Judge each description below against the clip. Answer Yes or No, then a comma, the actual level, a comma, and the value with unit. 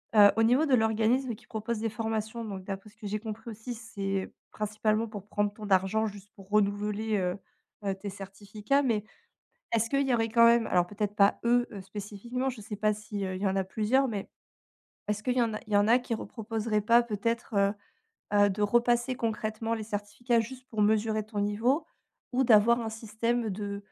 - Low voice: No, high, 215 Hz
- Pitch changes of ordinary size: No, narrow, 2.2 semitones